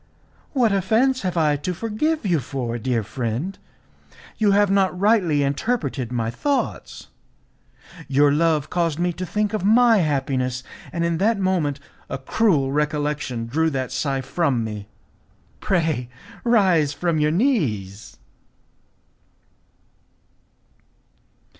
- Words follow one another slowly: Yes, slow, 120 wpm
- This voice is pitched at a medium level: Yes, medium, 160 Hz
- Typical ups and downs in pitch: No, wide, 6.6 semitones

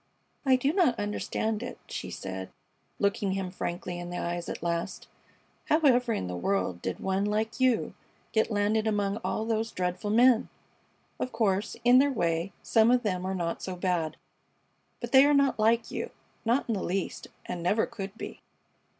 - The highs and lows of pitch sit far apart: No, average, 4.5 semitones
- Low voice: No, high, 205 Hz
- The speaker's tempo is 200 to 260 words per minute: No, average, 180 wpm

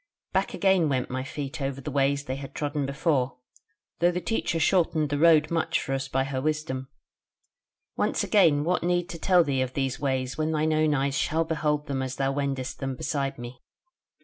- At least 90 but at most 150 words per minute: No, average, 200 wpm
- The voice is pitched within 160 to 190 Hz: No, medium, 145 Hz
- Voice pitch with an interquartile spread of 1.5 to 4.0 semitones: Yes, average, 2.9 semitones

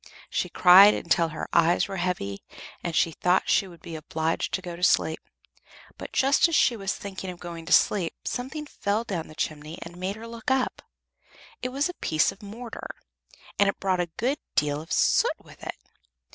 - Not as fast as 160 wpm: No, average, 200 wpm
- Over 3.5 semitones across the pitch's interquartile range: Yes, average, 4.7 semitones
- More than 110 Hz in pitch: Yes, medium, 185 Hz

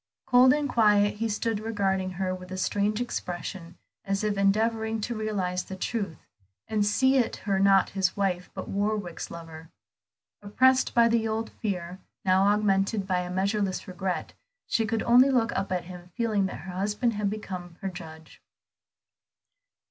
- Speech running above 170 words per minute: No, average, 165 wpm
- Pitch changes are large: No, average, 3.1 semitones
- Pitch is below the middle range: No, high, 200 Hz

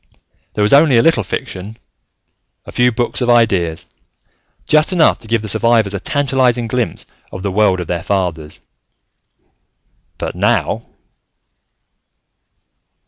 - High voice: No, low, 115 Hz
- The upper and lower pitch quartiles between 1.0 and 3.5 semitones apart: No, average, 4.4 semitones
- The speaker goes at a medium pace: No, slow, 130 wpm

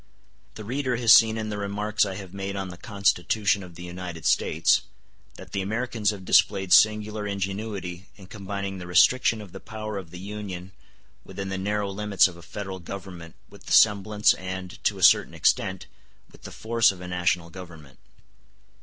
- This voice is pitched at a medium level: No, low, 100 Hz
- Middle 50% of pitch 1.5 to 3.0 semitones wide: Yes, narrow, 2.4 semitones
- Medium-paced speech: Yes, average, 180 wpm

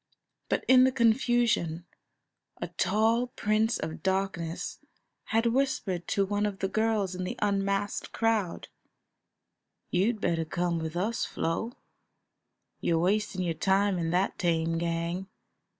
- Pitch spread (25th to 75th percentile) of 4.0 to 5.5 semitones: Yes, average, 4.3 semitones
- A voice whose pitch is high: Yes, high, 195 Hz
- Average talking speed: No, slow, 125 wpm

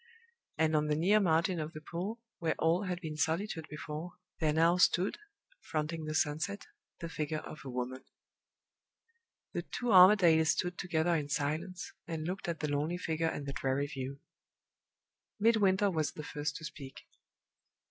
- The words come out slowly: No, average, 160 wpm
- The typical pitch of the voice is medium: Yes, medium, 160 Hz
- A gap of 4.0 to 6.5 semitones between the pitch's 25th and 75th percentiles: No, average, 2.9 semitones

